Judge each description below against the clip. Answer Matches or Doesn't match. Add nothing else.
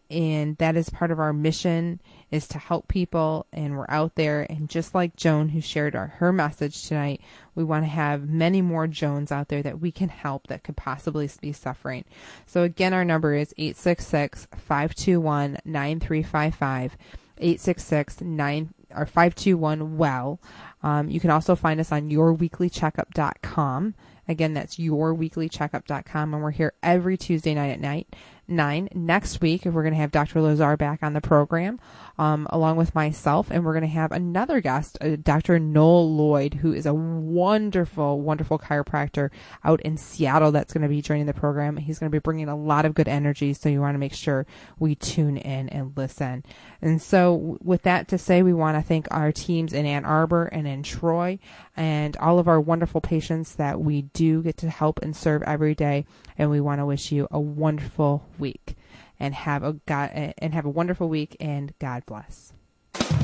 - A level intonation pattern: Matches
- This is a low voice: Doesn't match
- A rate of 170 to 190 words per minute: Matches